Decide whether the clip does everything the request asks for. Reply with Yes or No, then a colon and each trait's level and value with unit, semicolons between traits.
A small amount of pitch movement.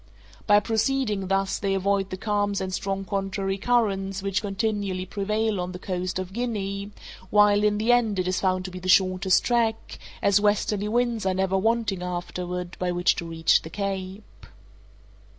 Yes: narrow, 2.1 semitones